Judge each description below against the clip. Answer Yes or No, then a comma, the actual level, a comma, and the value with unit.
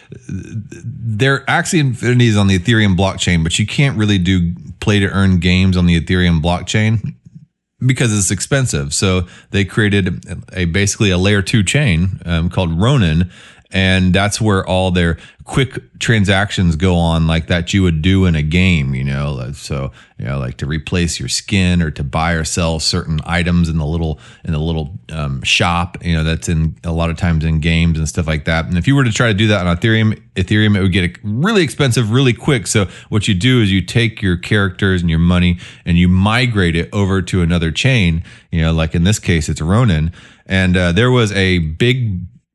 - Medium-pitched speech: No, very low, 95 Hz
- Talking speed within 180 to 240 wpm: Yes, average, 200 wpm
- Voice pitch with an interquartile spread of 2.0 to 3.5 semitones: No, average, 4.4 semitones